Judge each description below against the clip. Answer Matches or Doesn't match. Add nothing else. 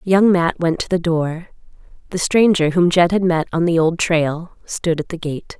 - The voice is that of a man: Doesn't match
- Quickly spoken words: Matches